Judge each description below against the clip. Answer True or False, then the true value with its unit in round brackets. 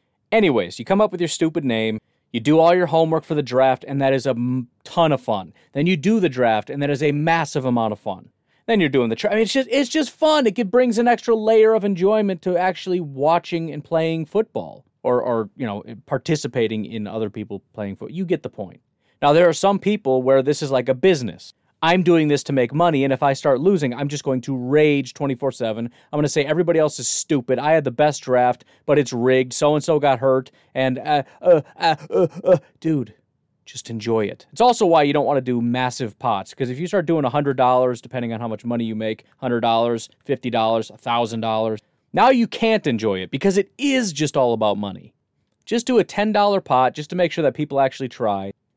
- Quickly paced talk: True (230 wpm)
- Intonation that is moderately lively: False (5.8 semitones)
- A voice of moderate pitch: True (145 Hz)